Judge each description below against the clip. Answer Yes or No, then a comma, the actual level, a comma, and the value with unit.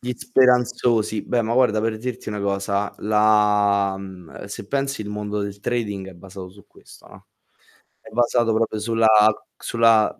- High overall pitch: No, low, 105 Hz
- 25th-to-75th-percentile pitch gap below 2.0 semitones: No, narrow, 2.6 semitones